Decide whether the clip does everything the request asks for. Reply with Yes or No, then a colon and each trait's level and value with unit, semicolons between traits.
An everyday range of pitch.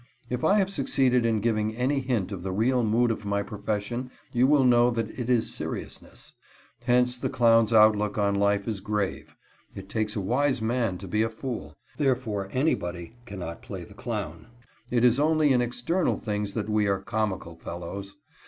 Yes: average, 3.5 semitones